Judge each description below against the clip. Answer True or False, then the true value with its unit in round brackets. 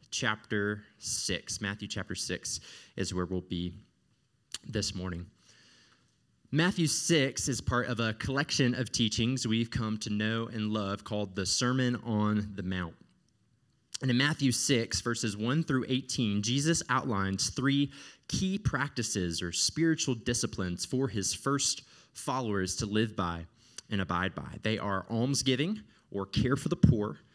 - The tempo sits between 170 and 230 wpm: False (145 wpm)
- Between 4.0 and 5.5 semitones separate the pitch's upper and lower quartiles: True (4.8 semitones)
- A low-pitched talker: True (110 Hz)